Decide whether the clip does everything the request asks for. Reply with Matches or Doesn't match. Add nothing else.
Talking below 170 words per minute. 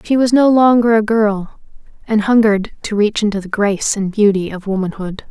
Doesn't match